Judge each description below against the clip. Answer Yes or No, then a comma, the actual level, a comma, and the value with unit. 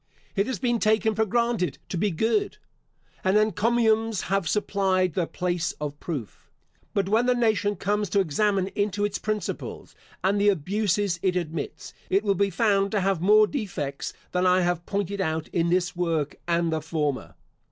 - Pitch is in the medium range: No, high, 195 Hz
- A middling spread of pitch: Yes, average, 3.4 semitones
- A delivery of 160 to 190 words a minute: Yes, average, 175 wpm